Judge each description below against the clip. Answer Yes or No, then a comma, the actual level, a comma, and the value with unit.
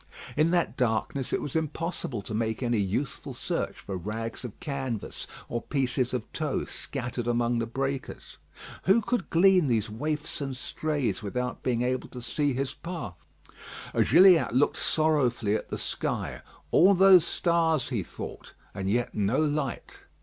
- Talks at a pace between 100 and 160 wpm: Yes, average, 155 wpm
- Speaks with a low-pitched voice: Yes, low, 130 Hz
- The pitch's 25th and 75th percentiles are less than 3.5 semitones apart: No, average, 5.0 semitones